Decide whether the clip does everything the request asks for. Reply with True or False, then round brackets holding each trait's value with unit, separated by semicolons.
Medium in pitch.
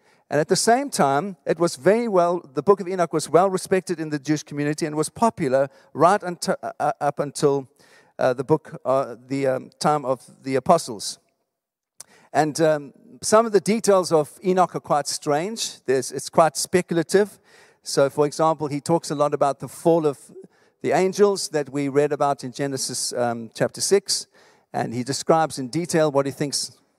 True (155 Hz)